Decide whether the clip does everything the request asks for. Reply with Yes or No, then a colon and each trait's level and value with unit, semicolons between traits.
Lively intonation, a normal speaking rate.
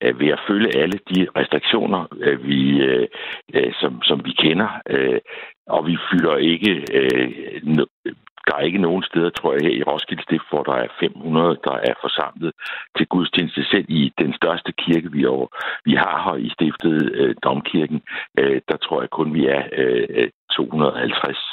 Yes: wide, 7.3 semitones; average, 155 wpm